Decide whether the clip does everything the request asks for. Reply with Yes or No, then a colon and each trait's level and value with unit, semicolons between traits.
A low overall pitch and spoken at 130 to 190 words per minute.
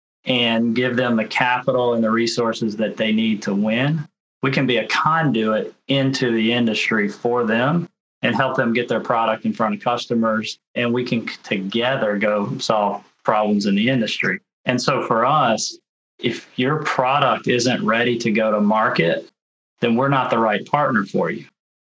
Yes: low, 115 Hz; average, 175 wpm